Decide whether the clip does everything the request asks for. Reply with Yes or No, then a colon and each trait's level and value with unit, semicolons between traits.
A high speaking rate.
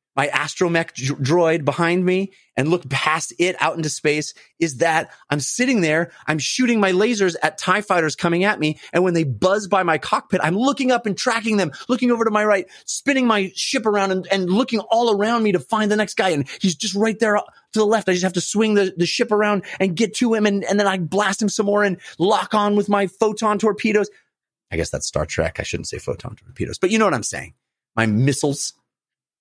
Yes: fast, 235 wpm